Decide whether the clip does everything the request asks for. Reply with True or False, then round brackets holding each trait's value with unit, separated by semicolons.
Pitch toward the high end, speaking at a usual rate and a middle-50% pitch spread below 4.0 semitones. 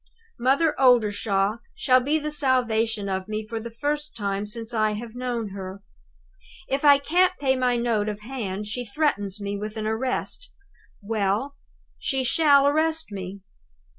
False (230 Hz; 155 wpm; 4.7 semitones)